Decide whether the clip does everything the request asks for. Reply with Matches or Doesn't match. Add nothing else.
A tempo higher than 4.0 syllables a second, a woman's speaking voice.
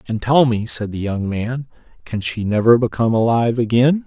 Doesn't match